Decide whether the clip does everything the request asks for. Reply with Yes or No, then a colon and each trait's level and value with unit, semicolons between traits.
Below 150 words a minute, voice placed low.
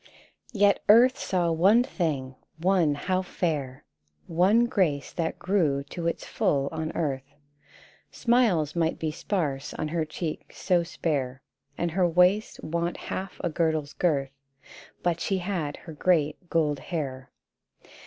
No: slow, 135 wpm; medium, 165 Hz